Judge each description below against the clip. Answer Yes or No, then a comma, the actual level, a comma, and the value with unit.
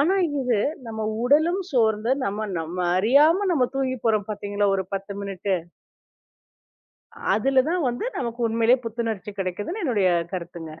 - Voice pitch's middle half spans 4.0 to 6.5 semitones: Yes, average, 4.7 semitones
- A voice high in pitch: Yes, high, 225 Hz